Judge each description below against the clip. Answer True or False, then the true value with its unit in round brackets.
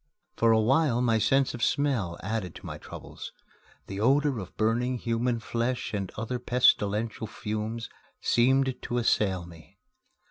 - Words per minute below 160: True (145 wpm)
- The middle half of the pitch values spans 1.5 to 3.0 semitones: True (2.7 semitones)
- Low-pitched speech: True (115 Hz)